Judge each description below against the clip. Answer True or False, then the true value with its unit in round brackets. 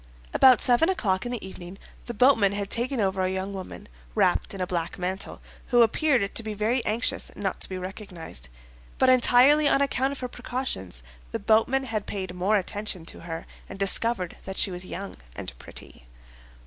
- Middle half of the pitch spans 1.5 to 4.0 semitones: False (4.6 semitones)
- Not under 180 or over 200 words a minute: True (185 wpm)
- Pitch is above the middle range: True (205 Hz)